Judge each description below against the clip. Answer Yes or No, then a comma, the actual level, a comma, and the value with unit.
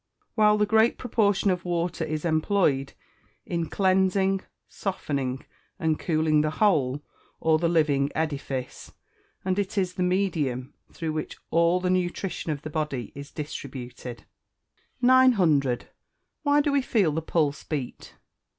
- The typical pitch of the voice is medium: Yes, medium, 165 Hz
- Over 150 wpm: No, slow, 135 wpm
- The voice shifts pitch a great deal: No, average, 4.7 semitones